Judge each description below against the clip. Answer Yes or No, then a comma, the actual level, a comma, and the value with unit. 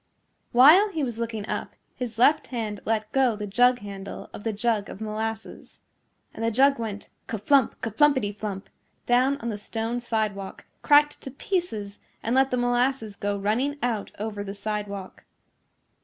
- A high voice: Yes, high, 225 Hz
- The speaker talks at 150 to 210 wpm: Yes, average, 170 wpm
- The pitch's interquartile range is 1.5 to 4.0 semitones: Yes, average, 3.5 semitones